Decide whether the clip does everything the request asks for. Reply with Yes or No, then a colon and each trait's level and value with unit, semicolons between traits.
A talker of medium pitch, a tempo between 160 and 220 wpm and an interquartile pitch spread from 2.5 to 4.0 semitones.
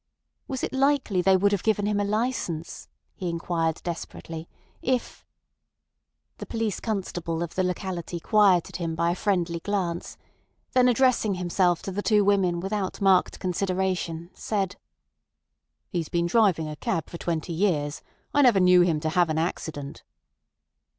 No: medium, 180 Hz; average, 150 wpm; average, 3.3 semitones